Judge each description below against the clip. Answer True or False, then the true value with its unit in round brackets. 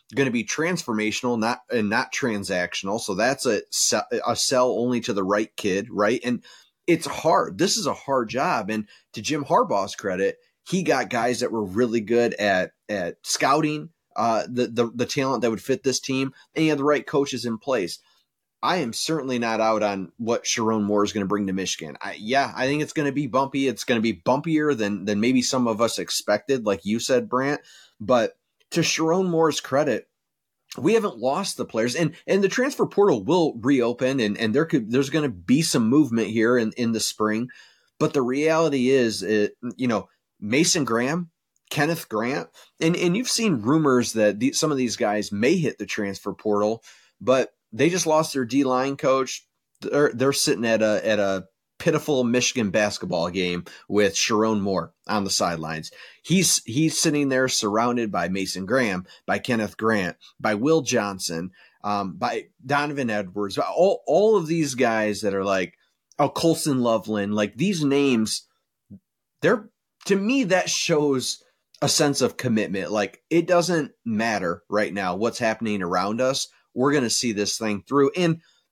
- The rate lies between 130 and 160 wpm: False (185 wpm)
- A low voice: True (125 Hz)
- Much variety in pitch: True (5.7 semitones)